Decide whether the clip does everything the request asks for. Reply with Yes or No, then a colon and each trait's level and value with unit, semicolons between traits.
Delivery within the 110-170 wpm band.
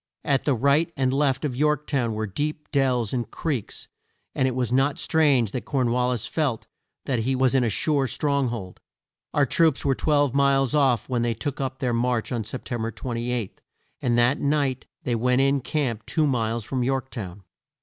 No: average, 200 wpm